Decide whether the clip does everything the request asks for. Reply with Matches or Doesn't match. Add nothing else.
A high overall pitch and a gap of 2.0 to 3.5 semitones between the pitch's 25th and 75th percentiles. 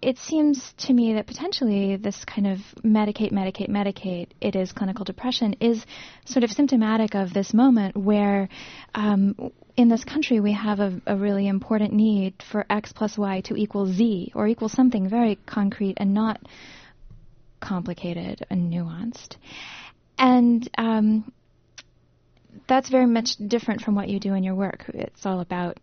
Matches